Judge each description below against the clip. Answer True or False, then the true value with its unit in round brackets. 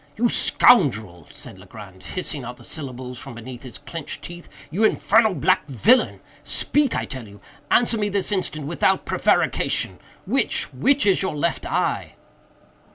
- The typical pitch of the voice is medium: True (155 Hz)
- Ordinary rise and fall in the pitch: False (8.7 semitones)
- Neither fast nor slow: False (130 wpm)